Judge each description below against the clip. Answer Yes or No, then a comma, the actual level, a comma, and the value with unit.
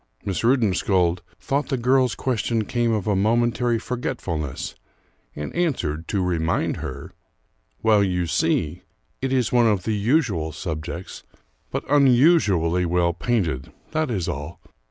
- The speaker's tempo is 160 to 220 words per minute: No, slow, 135 wpm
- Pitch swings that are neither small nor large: No, wide, 6.3 semitones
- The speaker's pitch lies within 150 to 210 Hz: No, low, 105 Hz